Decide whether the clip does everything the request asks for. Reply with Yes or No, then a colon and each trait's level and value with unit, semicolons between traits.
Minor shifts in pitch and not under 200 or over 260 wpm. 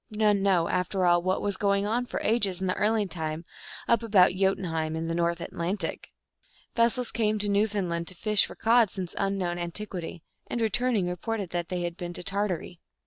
No: average, 3.3 semitones; fast, 205 wpm